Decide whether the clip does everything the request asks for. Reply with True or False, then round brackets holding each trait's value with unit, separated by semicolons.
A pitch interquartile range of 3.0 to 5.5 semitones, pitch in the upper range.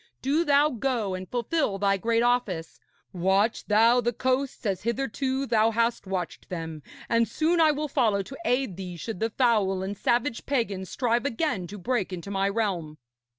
True (4.9 semitones; 225 Hz)